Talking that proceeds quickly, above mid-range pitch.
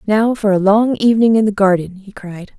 Yes: fast, 230 wpm; high, 205 Hz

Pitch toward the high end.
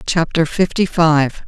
No: medium, 165 Hz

